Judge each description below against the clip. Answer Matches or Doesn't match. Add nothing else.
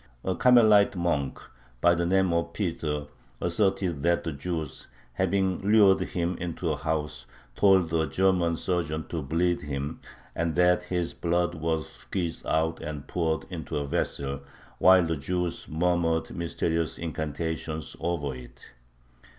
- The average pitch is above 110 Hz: Doesn't match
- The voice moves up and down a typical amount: Doesn't match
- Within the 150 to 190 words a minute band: Doesn't match